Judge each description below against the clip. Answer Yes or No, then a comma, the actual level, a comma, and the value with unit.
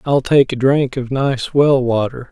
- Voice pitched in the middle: No, low, 130 Hz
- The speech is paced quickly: Yes, fast, 210 wpm